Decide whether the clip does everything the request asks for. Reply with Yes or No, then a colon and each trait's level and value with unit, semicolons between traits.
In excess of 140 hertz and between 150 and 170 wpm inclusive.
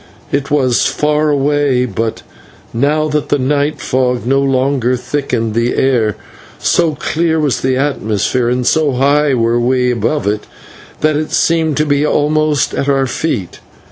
No: low, 135 Hz; average, 155 wpm